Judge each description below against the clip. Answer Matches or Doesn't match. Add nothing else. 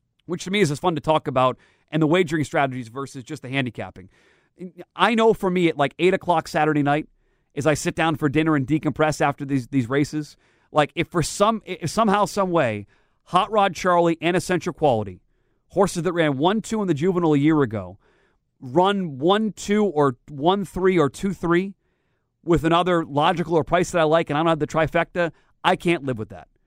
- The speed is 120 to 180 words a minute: Doesn't match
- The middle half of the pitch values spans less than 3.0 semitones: Doesn't match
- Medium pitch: Matches